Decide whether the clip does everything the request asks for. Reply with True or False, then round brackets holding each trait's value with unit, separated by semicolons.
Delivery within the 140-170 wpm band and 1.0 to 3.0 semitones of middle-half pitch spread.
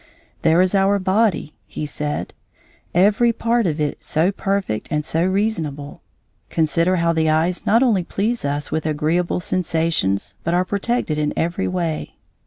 False (155 wpm; 4.1 semitones)